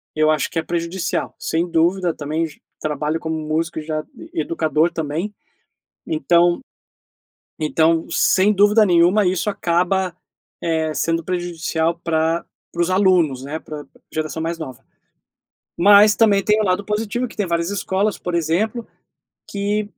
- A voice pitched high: No, medium, 170 Hz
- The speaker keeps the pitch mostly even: No, average, 3.6 semitones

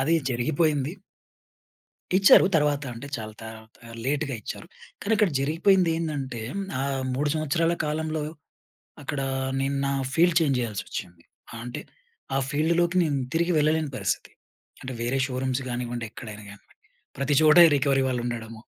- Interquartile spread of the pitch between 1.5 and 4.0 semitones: No, average, 4.6 semitones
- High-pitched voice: No, medium, 140 Hz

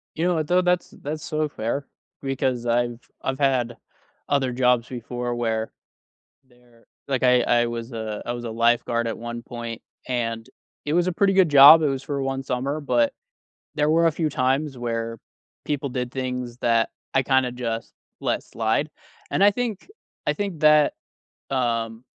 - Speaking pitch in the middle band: No, low, 125 Hz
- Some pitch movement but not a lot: Yes, average, 4.0 semitones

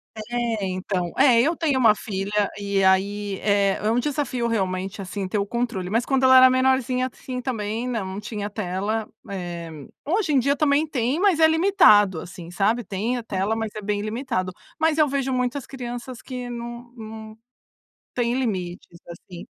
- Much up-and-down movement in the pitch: No, average, 4.5 semitones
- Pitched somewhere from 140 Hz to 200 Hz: No, high, 225 Hz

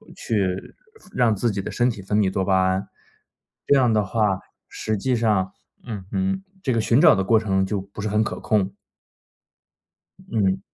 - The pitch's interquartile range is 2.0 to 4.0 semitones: Yes, average, 3.2 semitones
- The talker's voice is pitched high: No, low, 105 Hz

